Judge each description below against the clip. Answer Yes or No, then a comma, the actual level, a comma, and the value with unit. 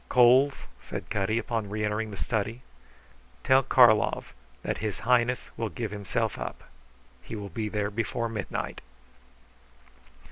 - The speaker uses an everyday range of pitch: No, narrow, 2.3 semitones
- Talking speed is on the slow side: Yes, slow, 130 wpm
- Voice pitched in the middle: No, low, 110 Hz